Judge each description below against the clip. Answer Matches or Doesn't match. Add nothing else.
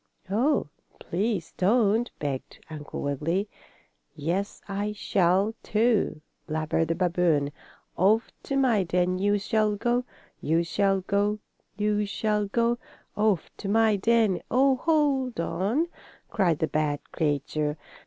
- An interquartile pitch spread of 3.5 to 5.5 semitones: Matches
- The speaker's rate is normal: Doesn't match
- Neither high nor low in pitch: Doesn't match